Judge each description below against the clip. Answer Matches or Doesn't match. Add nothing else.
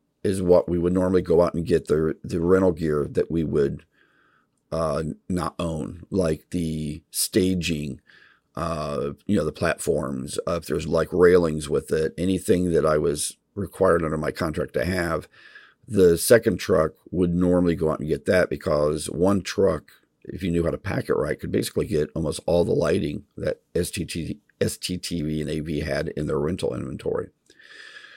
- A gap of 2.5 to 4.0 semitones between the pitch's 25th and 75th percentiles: Matches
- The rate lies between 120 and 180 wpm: Matches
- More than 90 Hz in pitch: Doesn't match